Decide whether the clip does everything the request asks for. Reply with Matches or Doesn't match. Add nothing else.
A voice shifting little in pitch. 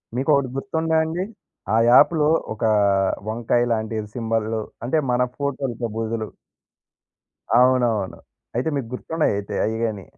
Doesn't match